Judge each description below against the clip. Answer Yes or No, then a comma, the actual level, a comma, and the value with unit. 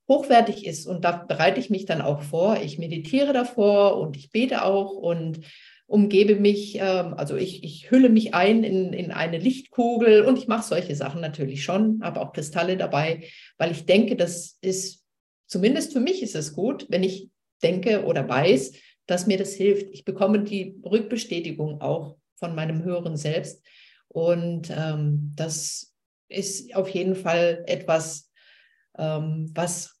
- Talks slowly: No, average, 160 wpm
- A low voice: No, medium, 180 Hz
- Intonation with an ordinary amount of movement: Yes, average, 4.1 semitones